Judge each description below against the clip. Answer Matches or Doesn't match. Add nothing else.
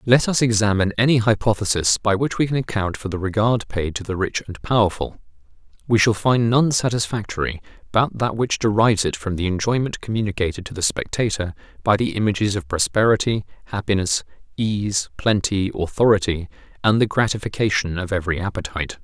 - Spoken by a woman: Doesn't match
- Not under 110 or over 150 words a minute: Doesn't match